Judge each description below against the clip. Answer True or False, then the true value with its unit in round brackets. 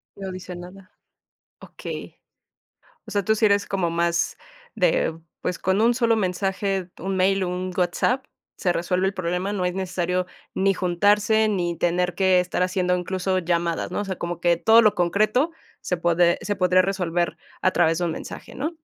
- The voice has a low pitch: False (185 Hz)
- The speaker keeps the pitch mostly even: True (2.1 semitones)